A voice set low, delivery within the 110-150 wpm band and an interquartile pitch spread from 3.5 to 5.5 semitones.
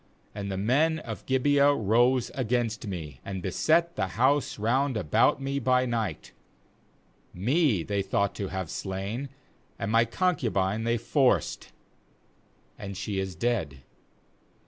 Yes: low, 115 Hz; average, 140 wpm; average, 5.2 semitones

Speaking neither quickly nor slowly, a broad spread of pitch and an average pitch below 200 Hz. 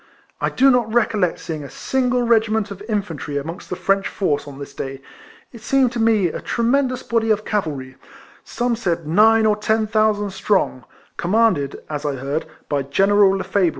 No: average, 185 wpm; wide, 5.9 semitones; high, 205 Hz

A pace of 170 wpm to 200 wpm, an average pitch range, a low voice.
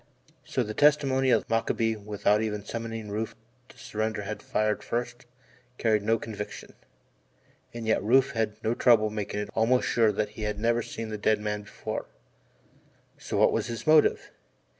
No: average, 180 wpm; narrow, 1.9 semitones; low, 110 Hz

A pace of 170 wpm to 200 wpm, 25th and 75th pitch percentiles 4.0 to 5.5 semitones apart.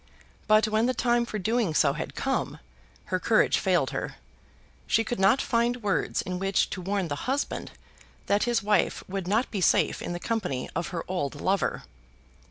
Yes: average, 180 wpm; average, 4.4 semitones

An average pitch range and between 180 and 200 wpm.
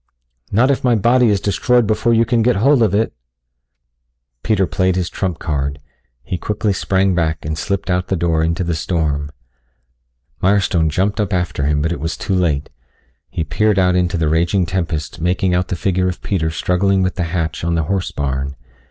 Yes: average, 3.5 semitones; average, 195 wpm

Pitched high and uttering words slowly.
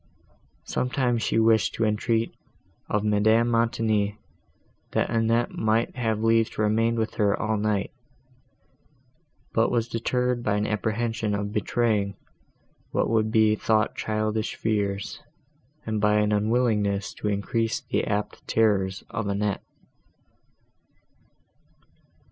No: low, 110 Hz; slow, 120 wpm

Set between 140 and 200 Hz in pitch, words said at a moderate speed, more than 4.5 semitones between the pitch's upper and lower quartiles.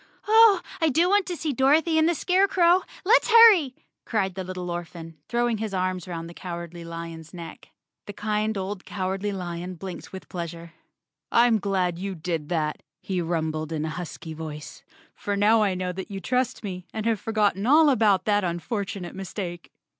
Yes: high, 190 Hz; average, 185 wpm; average, 5.2 semitones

